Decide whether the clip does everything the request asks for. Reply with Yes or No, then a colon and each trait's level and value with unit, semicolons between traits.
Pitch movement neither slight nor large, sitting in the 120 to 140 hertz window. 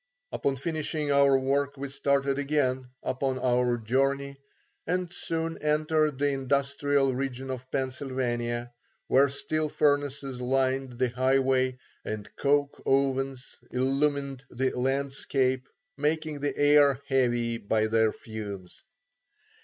No: narrow, 1.8 semitones; low, 135 Hz